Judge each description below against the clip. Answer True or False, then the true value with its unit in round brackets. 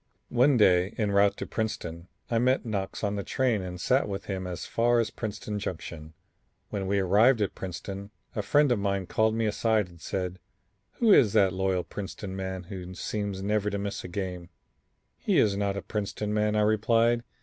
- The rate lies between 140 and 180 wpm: False (195 wpm)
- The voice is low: True (100 Hz)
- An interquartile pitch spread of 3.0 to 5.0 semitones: False (2.6 semitones)